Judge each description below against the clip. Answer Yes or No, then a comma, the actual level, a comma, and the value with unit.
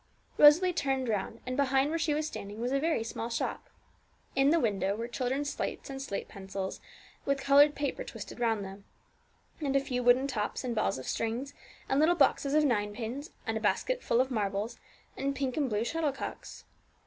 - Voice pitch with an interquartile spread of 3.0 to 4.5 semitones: Yes, average, 4.1 semitones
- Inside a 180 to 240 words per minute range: Yes, average, 190 wpm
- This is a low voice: No, very high, 260 Hz